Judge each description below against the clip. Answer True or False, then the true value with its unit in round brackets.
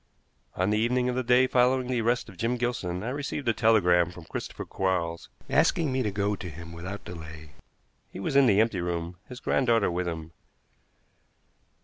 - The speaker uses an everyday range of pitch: False (5.9 semitones)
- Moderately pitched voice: False (105 Hz)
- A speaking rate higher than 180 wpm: True (190 wpm)